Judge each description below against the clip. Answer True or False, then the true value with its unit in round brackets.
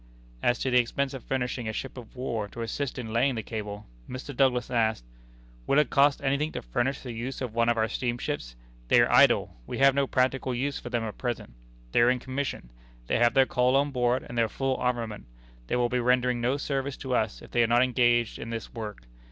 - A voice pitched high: False (125 Hz)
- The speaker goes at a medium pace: False (230 wpm)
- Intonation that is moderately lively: False (2.3 semitones)